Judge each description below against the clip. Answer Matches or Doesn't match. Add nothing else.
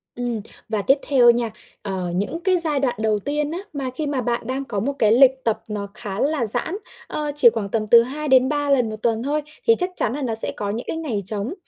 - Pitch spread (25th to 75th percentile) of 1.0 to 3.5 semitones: Doesn't match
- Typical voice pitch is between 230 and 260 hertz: Matches